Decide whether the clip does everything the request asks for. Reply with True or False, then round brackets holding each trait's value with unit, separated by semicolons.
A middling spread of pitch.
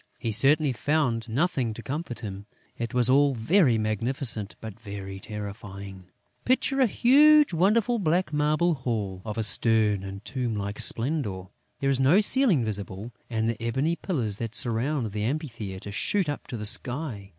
False (6.3 semitones)